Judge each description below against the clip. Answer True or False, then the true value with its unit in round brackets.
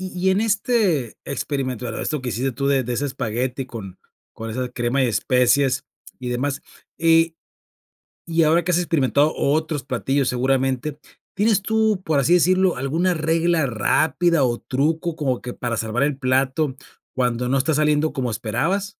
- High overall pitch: False (140 Hz)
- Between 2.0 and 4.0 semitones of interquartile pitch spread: False (4.5 semitones)